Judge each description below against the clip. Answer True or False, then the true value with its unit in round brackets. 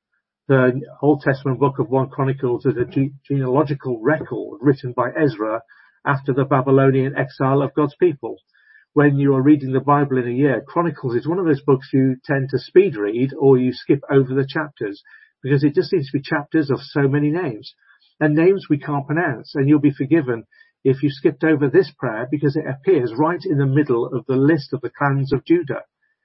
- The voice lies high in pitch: False (140 Hz)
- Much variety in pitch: False (2.7 semitones)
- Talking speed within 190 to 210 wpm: True (200 wpm)